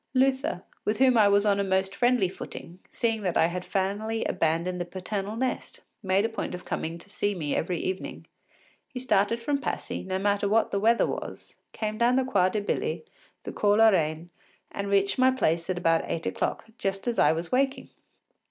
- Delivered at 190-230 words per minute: Yes, average, 200 wpm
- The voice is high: Yes, high, 200 Hz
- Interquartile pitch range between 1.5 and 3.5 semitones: No, average, 3.9 semitones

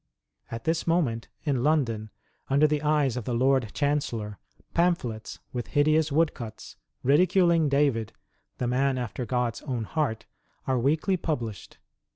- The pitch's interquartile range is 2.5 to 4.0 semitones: No, average, 4.8 semitones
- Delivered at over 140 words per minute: No, slow, 135 wpm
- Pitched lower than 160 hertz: Yes, low, 135 Hz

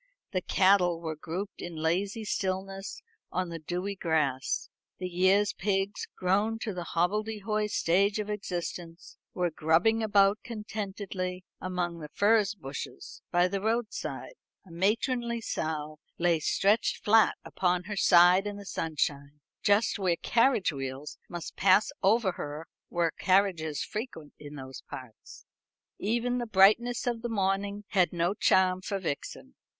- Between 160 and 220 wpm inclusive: No, average, 140 wpm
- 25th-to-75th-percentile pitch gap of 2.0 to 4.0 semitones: Yes, average, 3.6 semitones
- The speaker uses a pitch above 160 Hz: Yes, high, 190 Hz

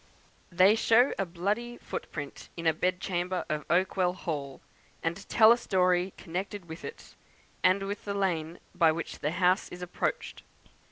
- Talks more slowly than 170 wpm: Yes, average, 160 wpm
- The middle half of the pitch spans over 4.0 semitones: No, average, 2.8 semitones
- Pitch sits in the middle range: Yes, medium, 180 Hz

